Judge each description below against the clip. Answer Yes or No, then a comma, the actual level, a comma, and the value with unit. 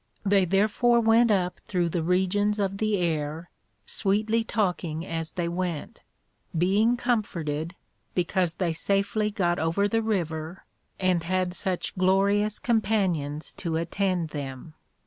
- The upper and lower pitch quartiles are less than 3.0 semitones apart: No, average, 3.7 semitones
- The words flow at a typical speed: No, slow, 125 wpm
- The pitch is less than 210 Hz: Yes, medium, 185 Hz